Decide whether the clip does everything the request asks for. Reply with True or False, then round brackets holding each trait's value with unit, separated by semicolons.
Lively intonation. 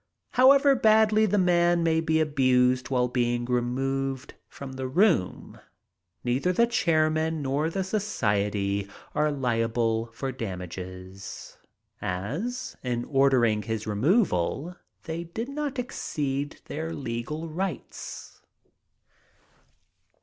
True (6.6 semitones)